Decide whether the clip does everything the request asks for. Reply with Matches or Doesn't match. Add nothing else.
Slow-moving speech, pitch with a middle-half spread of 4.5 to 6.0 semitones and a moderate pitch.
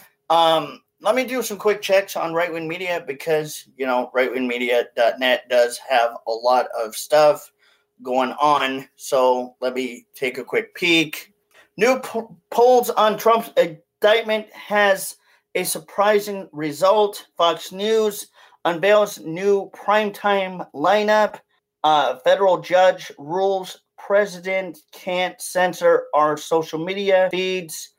Matches